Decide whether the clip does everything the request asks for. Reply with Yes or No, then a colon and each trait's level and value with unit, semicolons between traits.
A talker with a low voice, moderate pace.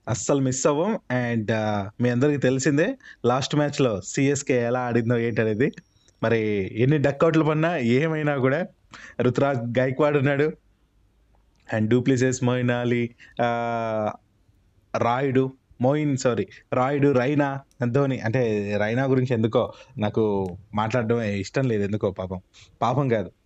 Yes: low, 125 Hz; average, 110 wpm